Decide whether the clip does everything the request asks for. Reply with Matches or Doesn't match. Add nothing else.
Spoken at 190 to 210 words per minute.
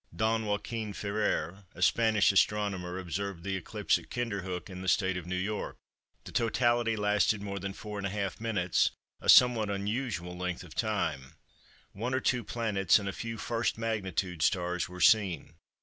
Doesn't match